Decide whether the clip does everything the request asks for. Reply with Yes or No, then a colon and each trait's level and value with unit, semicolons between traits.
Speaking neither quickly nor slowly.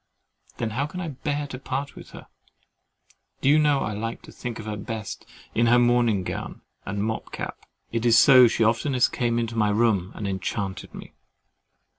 Yes: average, 190 wpm